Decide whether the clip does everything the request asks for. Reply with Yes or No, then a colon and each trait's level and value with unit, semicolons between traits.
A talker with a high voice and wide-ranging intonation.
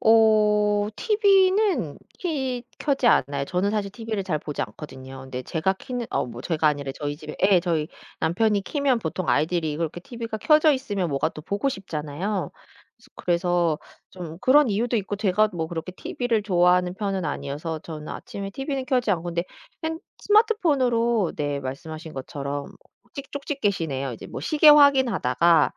Yes: high, 195 Hz; wide, 7.5 semitones